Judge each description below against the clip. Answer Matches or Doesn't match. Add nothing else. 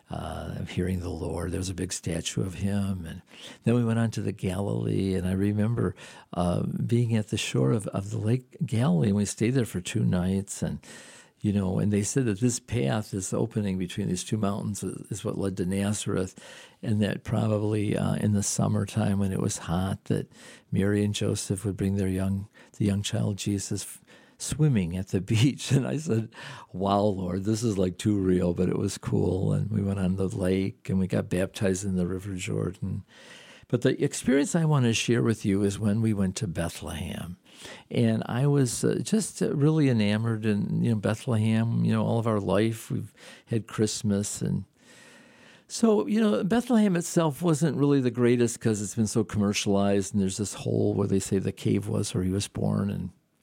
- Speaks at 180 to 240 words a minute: Matches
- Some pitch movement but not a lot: Matches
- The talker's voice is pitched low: Matches